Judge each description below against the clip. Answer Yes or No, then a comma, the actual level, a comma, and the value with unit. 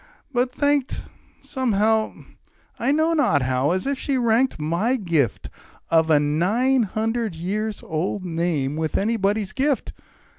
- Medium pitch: No, high, 210 Hz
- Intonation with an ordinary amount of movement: No, wide, 7.5 semitones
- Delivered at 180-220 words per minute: No, slow, 135 wpm